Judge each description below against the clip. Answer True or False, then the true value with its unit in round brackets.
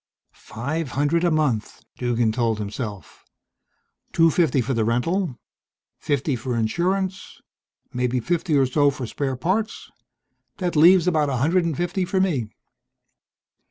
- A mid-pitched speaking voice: True (145 Hz)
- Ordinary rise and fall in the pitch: False (5.9 semitones)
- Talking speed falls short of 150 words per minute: True (135 wpm)